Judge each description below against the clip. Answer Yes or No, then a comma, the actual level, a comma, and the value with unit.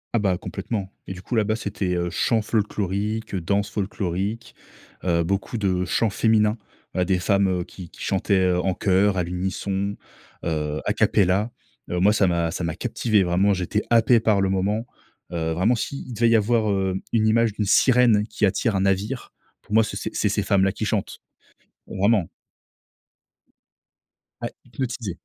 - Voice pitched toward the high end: No, low, 100 Hz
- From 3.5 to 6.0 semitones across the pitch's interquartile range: No, average, 2.9 semitones